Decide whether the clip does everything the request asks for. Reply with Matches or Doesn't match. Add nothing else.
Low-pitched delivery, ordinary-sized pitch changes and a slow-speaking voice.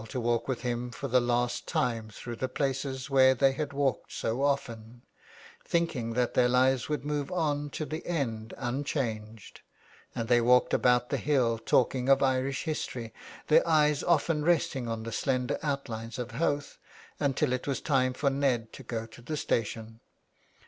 Doesn't match